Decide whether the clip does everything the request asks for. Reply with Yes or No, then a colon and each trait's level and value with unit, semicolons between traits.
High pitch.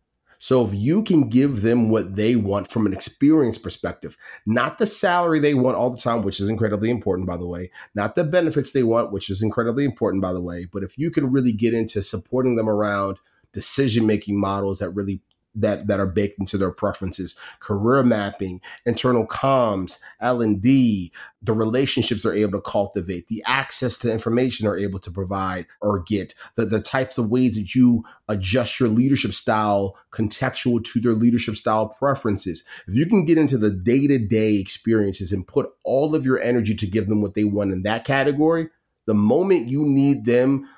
No: low, 110 Hz